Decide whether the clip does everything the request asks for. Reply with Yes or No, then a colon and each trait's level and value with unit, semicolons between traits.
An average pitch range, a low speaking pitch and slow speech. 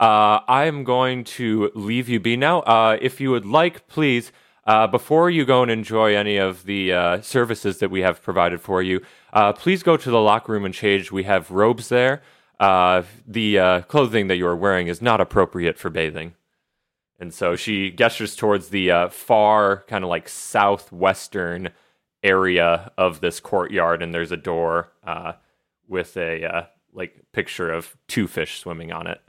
No: average, 4.4 semitones; low, 100 Hz; average, 185 wpm